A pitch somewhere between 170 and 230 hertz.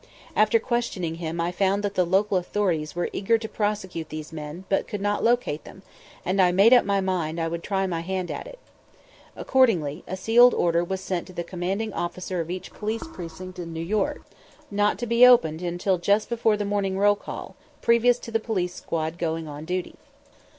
Yes: medium, 185 Hz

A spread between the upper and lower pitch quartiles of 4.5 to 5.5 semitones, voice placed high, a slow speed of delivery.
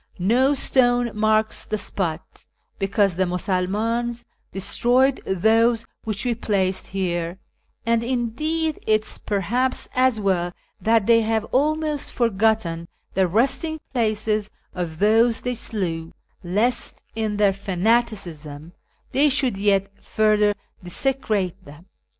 No: average, 4.0 semitones; high, 215 Hz; slow, 115 wpm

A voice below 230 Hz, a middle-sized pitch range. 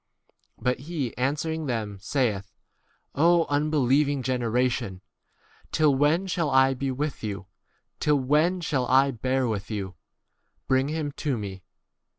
Yes: low, 135 Hz; average, 3.9 semitones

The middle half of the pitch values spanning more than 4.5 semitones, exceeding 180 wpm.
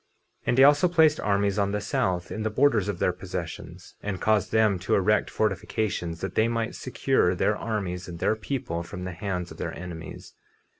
No: average, 3.4 semitones; average, 200 wpm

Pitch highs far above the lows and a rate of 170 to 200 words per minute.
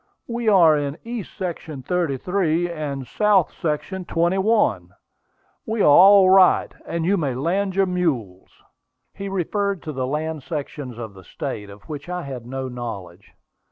No: wide, 6.2 semitones; average, 155 wpm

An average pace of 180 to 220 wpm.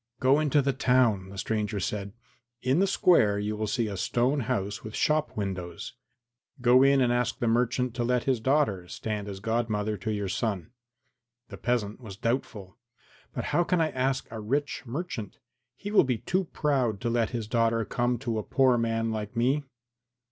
Yes: average, 185 wpm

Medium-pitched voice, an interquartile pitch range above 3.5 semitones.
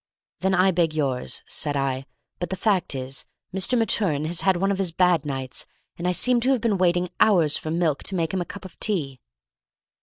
Yes: medium, 175 Hz; average, 4.2 semitones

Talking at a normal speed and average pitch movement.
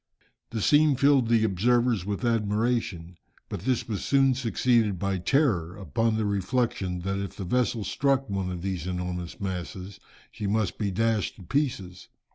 Yes: average, 160 wpm; average, 4.7 semitones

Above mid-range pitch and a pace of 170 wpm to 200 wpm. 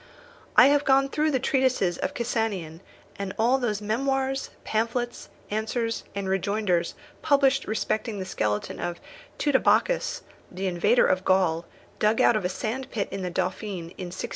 No: high, 215 Hz; average, 150 wpm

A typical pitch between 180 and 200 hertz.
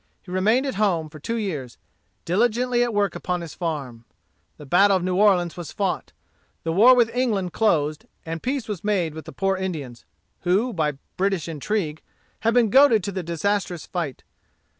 Yes: medium, 185 Hz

